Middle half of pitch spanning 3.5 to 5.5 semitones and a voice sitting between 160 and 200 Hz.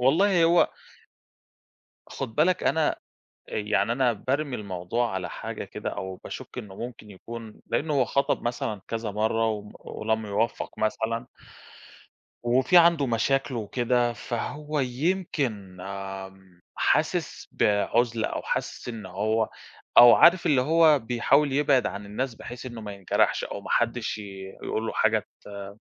No: average, 4.2 semitones; low, 120 Hz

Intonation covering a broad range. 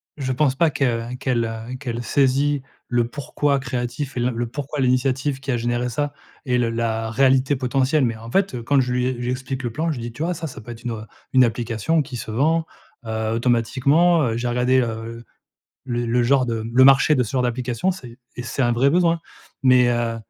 No: average, 2.7 semitones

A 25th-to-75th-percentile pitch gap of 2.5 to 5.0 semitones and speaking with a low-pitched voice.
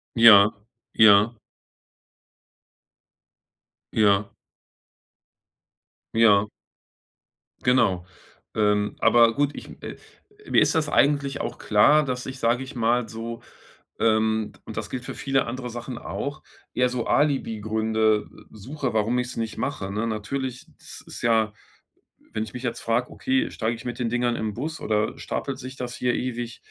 Yes: average, 2.8 semitones; low, 115 Hz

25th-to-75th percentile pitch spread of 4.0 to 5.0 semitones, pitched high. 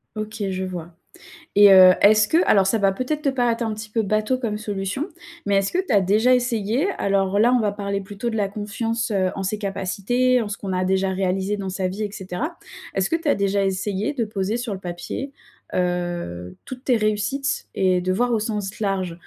No: average, 3.2 semitones; high, 205 Hz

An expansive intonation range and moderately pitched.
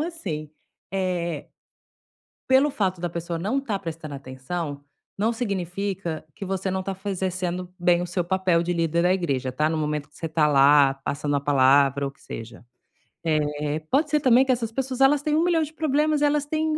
Yes: wide, 7.9 semitones; medium, 180 Hz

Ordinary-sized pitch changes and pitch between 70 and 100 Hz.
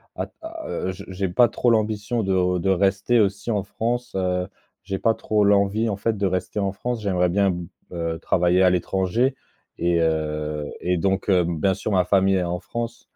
Yes: average, 3.0 semitones; very low, 95 Hz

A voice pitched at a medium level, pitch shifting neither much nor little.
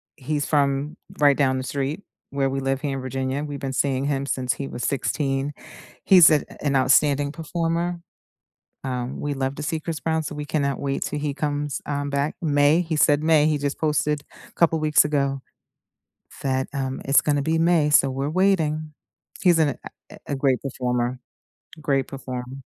No: medium, 145 Hz; narrow, 2.0 semitones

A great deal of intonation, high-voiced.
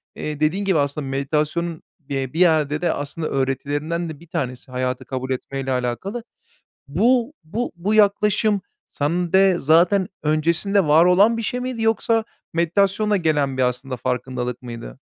No: wide, 6.3 semitones; medium, 160 Hz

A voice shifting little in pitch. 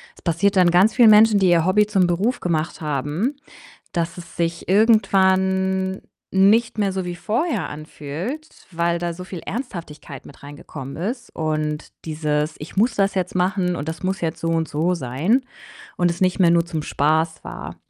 No: average, 3.4 semitones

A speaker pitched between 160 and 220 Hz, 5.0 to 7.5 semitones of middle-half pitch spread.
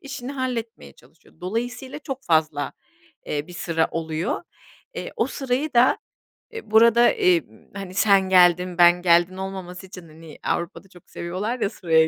Yes: medium, 185 Hz; wide, 5.6 semitones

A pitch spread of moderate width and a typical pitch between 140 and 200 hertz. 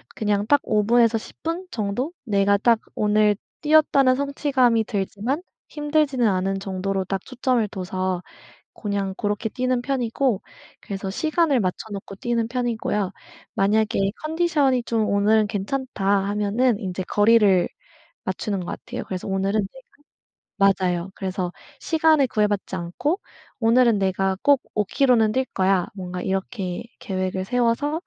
No: average, 4.7 semitones; high, 215 Hz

